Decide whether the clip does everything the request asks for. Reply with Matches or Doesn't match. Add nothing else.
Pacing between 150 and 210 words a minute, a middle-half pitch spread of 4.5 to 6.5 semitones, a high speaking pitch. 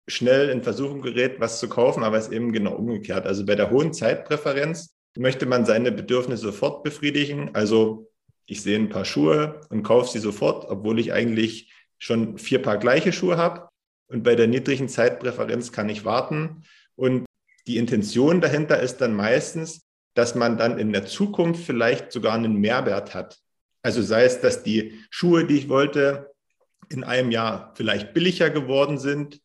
Doesn't match